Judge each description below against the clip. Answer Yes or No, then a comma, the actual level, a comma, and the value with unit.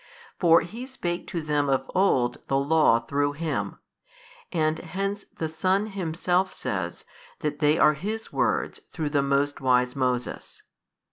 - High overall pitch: No, medium, 155 Hz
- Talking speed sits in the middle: Yes, average, 150 wpm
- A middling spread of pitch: Yes, average, 4.5 semitones